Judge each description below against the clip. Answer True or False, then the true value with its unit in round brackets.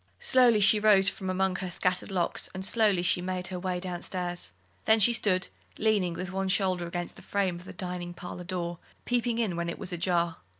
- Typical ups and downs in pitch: False (2.0 semitones)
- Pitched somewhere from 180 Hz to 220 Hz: True (185 Hz)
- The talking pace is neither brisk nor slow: False (210 wpm)